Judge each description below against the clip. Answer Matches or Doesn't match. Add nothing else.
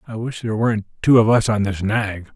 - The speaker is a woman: Doesn't match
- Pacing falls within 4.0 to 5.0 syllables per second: Doesn't match